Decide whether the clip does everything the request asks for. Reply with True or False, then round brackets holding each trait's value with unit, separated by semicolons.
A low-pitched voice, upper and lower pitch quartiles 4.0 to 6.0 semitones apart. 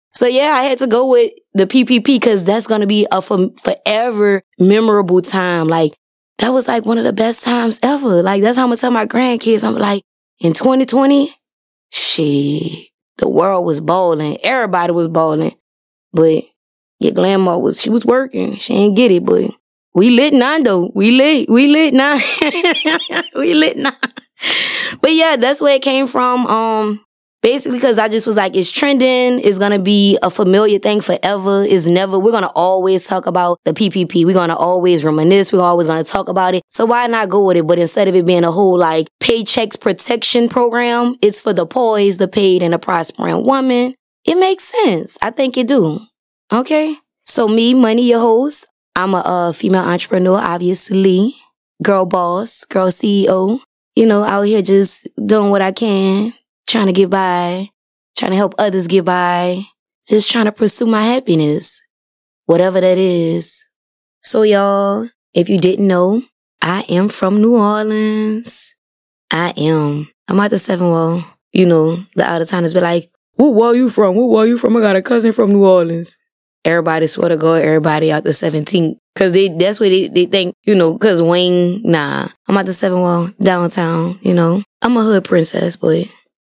False (200 Hz; 4.8 semitones)